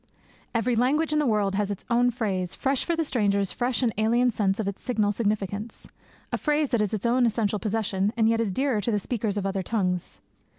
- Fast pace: Yes, fast, 220 wpm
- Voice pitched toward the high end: Yes, high, 220 Hz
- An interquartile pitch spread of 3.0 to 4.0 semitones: Yes, average, 3.3 semitones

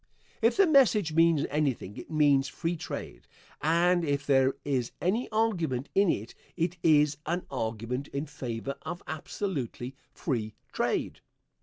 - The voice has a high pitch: No, medium, 150 Hz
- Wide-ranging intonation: No, average, 4.7 semitones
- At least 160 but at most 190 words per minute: No, average, 140 wpm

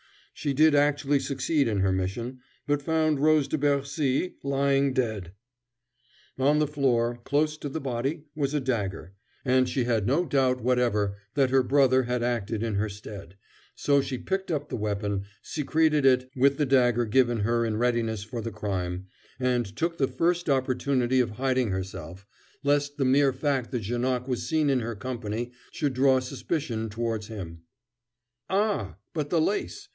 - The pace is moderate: Yes, average, 170 wpm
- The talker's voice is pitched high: No, low, 130 Hz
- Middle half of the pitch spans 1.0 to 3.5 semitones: No, average, 3.9 semitones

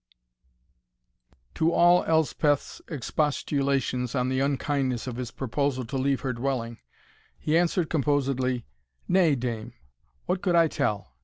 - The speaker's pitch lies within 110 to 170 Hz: Yes, low, 135 Hz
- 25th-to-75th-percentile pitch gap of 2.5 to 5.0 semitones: Yes, average, 3.6 semitones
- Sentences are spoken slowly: Yes, slow, 125 wpm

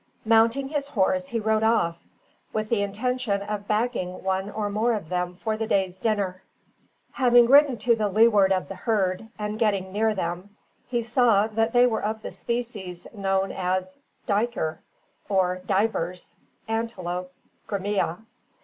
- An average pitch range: Yes, average, 3.3 semitones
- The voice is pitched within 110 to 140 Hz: No, high, 210 Hz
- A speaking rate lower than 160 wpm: Yes, average, 150 wpm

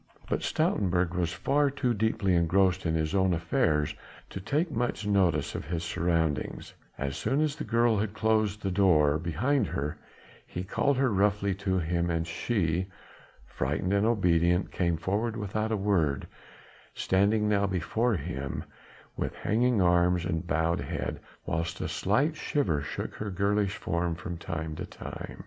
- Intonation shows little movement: No, average, 4.3 semitones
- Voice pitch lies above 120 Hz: No, very low, 95 Hz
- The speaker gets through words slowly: No, average, 160 wpm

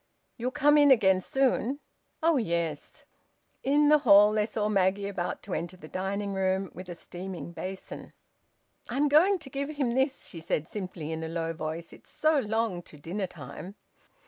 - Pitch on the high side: Yes, high, 200 Hz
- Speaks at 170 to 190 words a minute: Yes, average, 175 wpm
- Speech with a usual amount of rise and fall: No, wide, 7.3 semitones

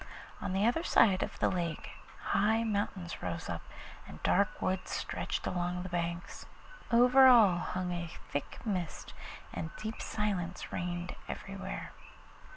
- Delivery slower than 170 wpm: Yes, average, 140 wpm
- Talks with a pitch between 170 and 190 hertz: Yes, medium, 185 Hz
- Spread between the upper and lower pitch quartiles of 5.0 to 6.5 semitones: No, average, 3.3 semitones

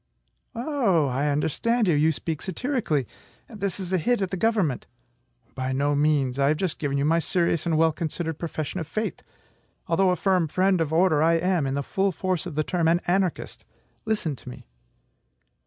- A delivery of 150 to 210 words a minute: Yes, average, 190 wpm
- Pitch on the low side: No, medium, 165 Hz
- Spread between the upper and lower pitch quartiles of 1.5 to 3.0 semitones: No, average, 4.1 semitones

